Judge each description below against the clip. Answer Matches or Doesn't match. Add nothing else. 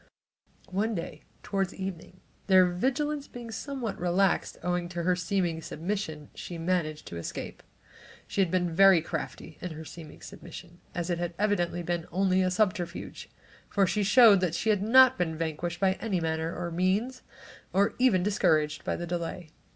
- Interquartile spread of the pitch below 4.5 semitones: Matches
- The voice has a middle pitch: Matches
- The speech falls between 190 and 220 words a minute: Doesn't match